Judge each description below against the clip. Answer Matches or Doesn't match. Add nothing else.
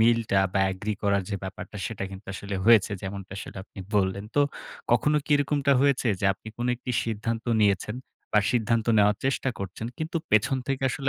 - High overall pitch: Doesn't match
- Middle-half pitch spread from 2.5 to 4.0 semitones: Matches